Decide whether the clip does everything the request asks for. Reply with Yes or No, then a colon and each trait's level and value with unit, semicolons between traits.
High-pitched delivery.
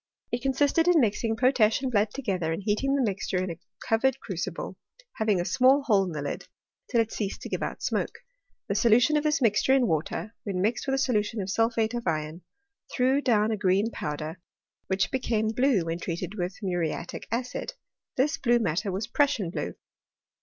Yes: high, 220 Hz